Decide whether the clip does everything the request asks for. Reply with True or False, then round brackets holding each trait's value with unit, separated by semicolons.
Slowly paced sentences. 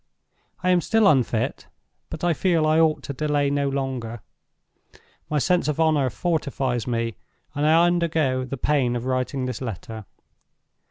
False (155 wpm)